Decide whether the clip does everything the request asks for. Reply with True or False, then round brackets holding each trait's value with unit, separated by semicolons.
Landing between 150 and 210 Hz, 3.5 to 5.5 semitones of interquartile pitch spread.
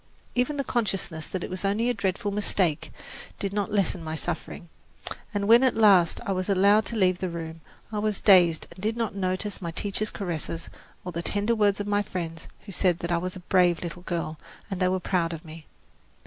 False (185 Hz; 3.1 semitones)